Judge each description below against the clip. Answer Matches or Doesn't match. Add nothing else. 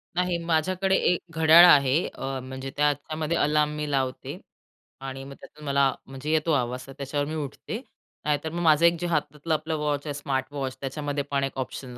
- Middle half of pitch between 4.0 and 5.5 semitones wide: Doesn't match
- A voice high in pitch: Doesn't match